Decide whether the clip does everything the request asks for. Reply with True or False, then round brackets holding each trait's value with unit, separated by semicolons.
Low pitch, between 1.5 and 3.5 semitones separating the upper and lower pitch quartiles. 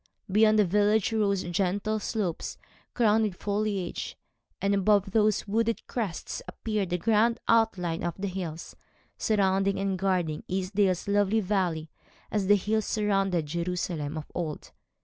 False (195 Hz; 2.9 semitones)